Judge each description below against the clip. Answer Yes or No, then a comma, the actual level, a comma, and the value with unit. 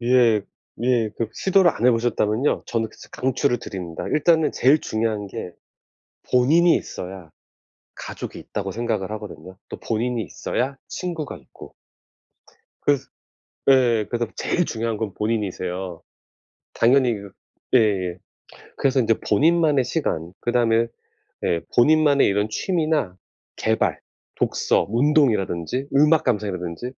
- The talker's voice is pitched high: No, low, 115 Hz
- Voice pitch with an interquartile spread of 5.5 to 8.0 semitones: No, average, 5.1 semitones